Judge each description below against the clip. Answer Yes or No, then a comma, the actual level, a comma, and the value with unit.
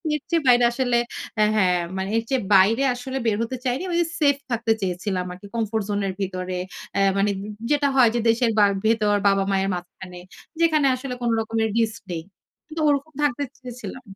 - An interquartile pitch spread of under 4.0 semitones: No, average, 4.9 semitones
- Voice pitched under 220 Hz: No, high, 225 Hz